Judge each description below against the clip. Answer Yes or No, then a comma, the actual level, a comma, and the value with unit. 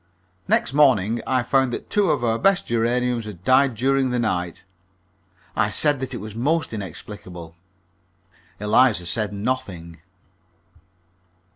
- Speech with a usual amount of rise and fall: Yes, average, 4.2 semitones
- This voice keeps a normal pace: No, slow, 130 wpm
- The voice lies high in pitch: No, low, 115 Hz